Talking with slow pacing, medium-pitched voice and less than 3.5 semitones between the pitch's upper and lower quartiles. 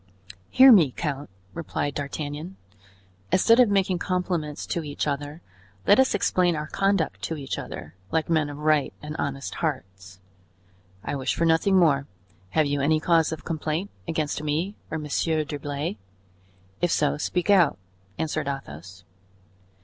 No: average, 150 wpm; medium, 155 Hz; average, 3.1 semitones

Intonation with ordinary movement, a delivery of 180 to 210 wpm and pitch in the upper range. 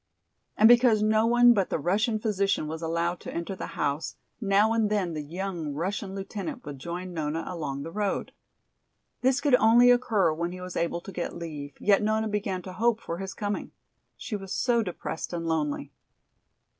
Yes: average, 4.5 semitones; average, 185 wpm; high, 195 Hz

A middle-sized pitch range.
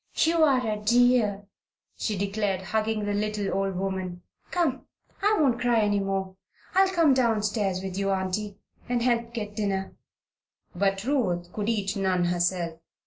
Yes: average, 3.6 semitones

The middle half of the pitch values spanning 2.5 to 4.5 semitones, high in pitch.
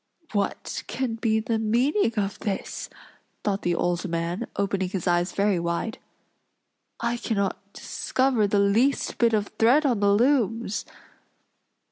Yes: average, 3.2 semitones; high, 210 Hz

